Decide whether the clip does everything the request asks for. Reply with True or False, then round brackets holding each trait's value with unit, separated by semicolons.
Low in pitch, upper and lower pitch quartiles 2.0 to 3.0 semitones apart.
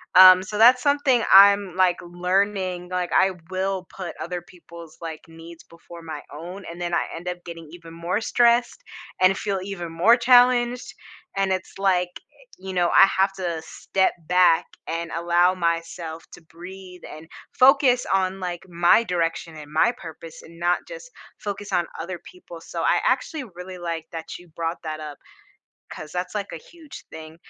False (180 Hz; 2.7 semitones)